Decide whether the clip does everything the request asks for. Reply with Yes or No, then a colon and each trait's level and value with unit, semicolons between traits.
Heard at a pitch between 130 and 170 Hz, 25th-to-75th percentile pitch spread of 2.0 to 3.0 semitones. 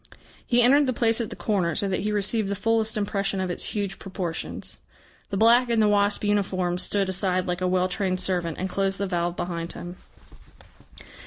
No: high, 195 Hz; narrow, 2.6 semitones